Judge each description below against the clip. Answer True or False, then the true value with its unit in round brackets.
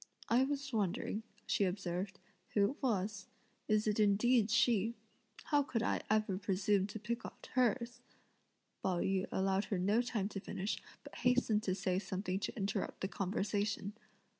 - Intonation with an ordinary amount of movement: True (3.3 semitones)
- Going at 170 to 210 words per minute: False (160 wpm)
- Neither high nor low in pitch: False (205 Hz)